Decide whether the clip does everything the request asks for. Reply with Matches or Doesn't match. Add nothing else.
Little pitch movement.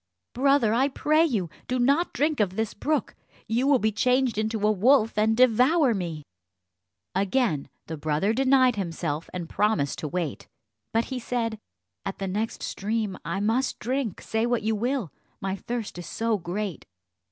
Doesn't match